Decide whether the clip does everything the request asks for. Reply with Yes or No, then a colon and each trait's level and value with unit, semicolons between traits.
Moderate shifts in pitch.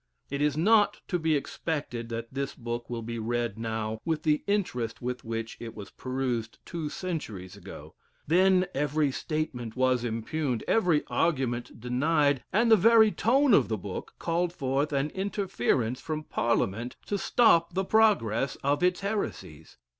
No: wide, 6.7 semitones